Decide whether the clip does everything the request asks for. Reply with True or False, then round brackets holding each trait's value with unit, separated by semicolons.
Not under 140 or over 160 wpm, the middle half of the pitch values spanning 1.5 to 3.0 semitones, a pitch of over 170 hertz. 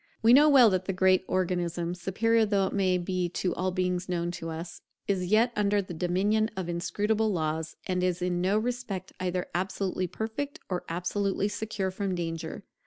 False (175 wpm; 2.7 semitones; 185 Hz)